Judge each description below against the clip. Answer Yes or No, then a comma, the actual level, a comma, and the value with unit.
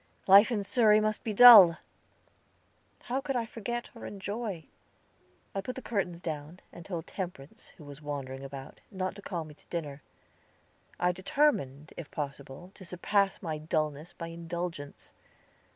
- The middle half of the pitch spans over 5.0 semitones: Yes, wide, 5.5 semitones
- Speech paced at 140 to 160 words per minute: Yes, average, 150 wpm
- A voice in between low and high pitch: Yes, medium, 175 Hz